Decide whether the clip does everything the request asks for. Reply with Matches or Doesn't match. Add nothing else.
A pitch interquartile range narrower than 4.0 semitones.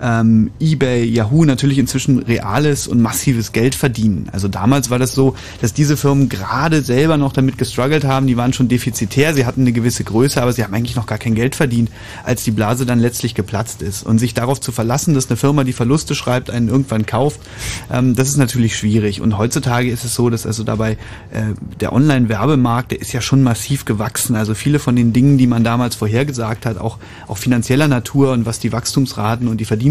Matches